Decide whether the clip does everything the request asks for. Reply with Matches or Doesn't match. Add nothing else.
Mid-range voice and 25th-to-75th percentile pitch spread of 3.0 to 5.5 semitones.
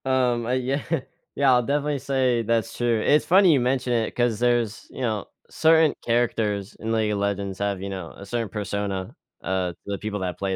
Doesn't match